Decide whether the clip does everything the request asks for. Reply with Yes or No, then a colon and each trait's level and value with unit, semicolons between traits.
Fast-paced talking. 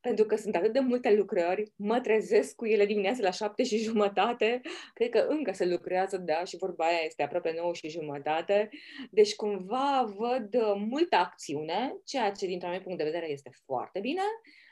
Yes: fast, 185 wpm